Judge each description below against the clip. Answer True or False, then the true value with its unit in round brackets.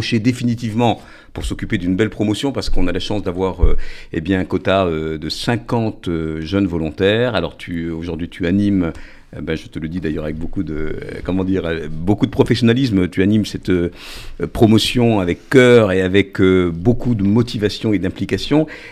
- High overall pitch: False (95 Hz)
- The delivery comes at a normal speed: True (180 wpm)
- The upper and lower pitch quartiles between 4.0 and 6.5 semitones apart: True (4.5 semitones)